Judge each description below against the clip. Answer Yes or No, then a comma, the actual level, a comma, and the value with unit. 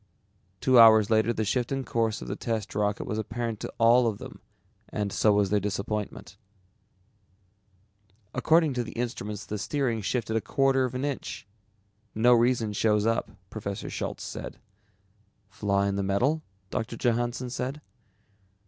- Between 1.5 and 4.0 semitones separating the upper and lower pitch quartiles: Yes, average, 3.1 semitones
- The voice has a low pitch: Yes, low, 115 Hz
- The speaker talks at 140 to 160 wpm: Yes, average, 155 wpm